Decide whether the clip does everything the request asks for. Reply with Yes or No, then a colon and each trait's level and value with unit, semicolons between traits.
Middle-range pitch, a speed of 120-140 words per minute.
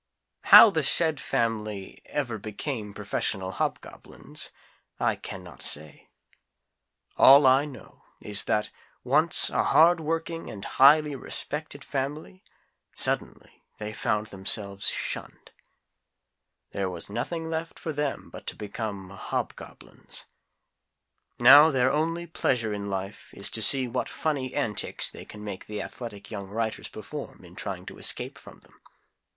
No: low, 120 Hz; slow, 135 wpm